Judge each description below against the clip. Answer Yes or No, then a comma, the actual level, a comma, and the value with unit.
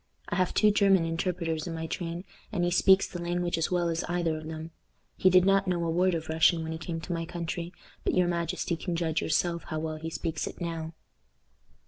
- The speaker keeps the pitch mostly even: Yes, narrow, 1.6 semitones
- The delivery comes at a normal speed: No, fast, 225 wpm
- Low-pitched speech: No, medium, 170 Hz